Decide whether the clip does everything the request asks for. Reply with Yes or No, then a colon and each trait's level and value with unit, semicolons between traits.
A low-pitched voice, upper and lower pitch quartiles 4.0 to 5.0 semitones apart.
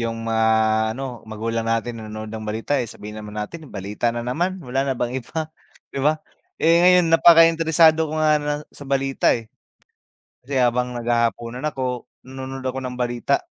Yes: low, 125 Hz; average, 4.7 semitones